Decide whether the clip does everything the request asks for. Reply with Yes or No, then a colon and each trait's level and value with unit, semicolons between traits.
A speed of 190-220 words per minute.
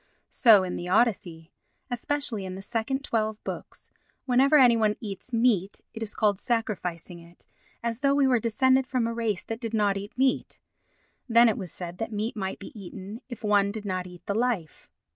Yes: average, 195 wpm